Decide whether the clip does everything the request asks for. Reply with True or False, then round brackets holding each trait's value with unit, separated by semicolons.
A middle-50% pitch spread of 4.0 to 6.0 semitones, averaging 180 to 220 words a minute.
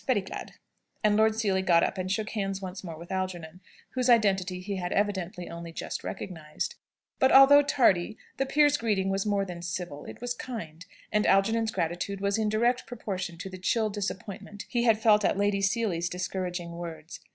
False (3.5 semitones; 185 wpm)